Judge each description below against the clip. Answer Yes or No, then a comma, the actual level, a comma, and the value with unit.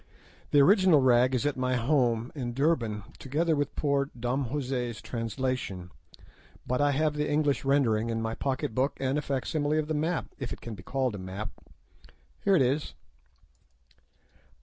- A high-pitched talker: No, low, 135 Hz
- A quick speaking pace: No, average, 170 wpm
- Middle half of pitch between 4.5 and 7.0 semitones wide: No, average, 3.6 semitones